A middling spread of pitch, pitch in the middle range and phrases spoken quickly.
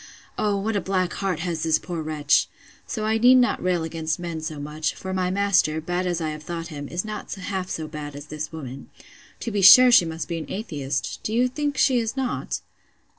Yes: average, 4.6 semitones; medium, 175 Hz; fast, 215 wpm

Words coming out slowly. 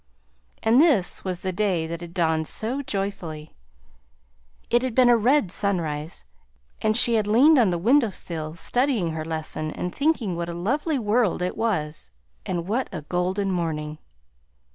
No: average, 165 wpm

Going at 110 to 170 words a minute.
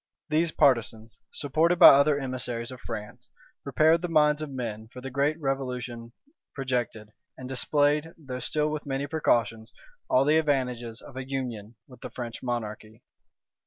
Yes: average, 155 wpm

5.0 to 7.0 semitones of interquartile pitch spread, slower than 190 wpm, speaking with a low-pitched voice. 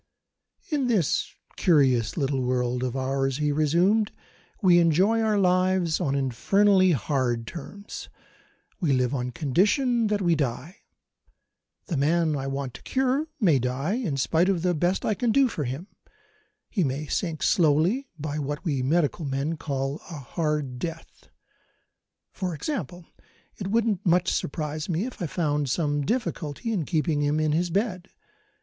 No: average, 5.3 semitones; average, 155 wpm; medium, 160 Hz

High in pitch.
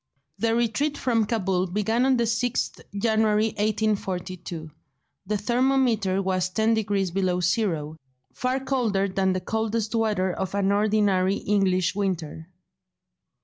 Yes: high, 205 Hz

